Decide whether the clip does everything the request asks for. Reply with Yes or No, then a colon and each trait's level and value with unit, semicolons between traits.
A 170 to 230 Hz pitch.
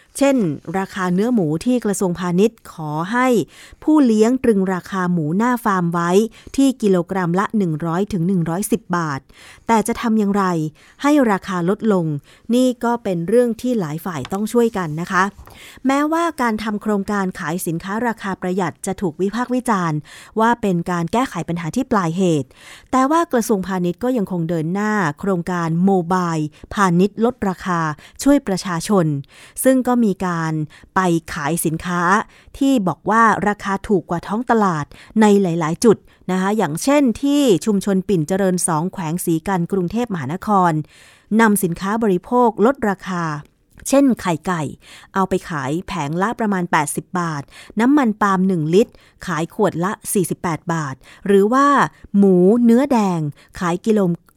Yes: high, 190 Hz